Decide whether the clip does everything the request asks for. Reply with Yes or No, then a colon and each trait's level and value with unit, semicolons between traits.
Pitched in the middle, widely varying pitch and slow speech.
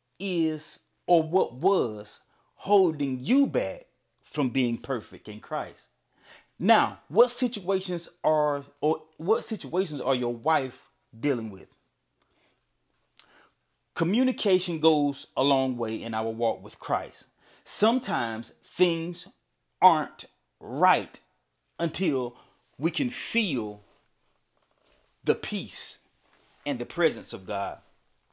Yes: medium, 155 Hz; wide, 7.9 semitones; slow, 105 wpm